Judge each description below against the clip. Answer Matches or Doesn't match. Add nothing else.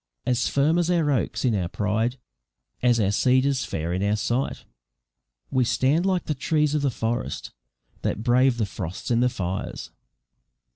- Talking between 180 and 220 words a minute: Doesn't match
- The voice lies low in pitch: Matches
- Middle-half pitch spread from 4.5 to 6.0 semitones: Matches